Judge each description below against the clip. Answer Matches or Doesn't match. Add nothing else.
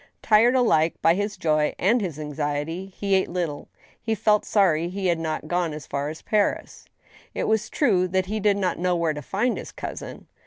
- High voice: Doesn't match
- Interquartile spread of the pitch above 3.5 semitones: Matches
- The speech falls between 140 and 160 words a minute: Doesn't match